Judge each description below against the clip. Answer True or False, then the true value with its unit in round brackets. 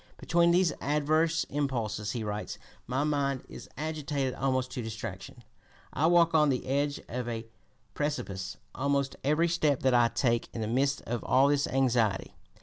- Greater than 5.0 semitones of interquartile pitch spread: False (3.9 semitones)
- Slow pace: False (165 wpm)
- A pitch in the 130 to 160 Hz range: True (135 Hz)